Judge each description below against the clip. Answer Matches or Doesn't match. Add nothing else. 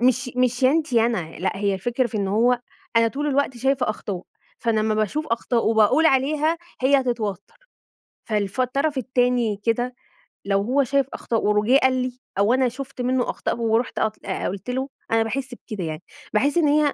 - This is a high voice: Matches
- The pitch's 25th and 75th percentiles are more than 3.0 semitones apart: Matches